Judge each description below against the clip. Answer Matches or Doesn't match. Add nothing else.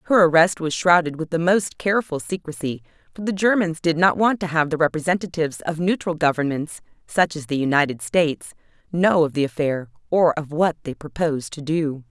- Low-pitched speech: Doesn't match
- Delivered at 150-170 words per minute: Doesn't match